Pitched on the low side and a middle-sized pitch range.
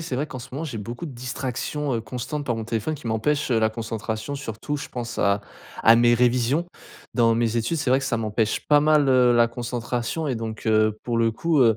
Yes: low, 120 Hz; average, 3.4 semitones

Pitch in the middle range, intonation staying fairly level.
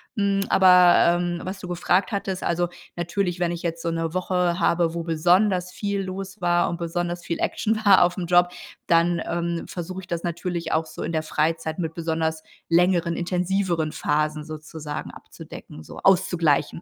Yes: medium, 175 Hz; narrow, 1.7 semitones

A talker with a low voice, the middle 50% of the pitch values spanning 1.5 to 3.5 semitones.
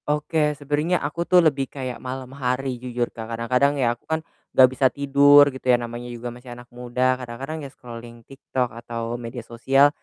Yes: low, 130 Hz; average, 2.8 semitones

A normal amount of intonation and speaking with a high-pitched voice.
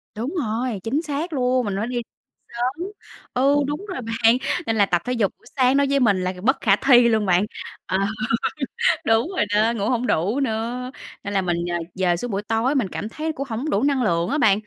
Yes: average, 4.5 semitones; high, 235 Hz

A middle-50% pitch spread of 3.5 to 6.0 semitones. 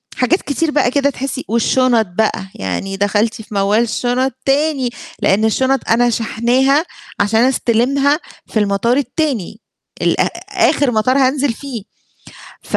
Yes: average, 3.8 semitones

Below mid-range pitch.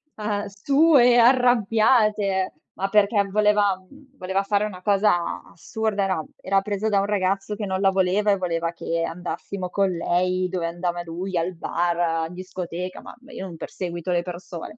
No: high, 190 Hz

